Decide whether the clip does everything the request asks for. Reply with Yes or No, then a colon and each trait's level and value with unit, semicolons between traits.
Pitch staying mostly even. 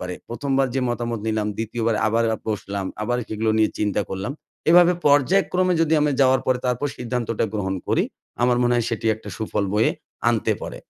No: average, 3.3 semitones